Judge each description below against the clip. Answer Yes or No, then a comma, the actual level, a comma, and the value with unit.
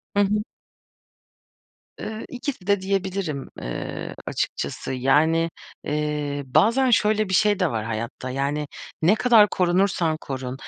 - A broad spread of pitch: Yes, wide, 6.4 semitones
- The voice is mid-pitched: Yes, medium, 170 Hz